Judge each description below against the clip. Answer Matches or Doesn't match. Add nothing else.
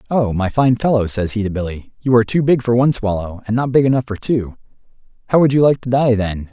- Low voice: Matches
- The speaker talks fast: Matches